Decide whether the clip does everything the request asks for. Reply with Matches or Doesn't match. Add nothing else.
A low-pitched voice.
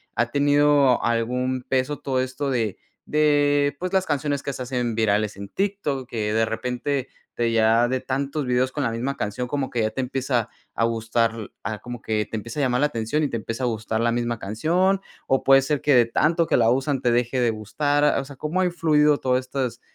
Matches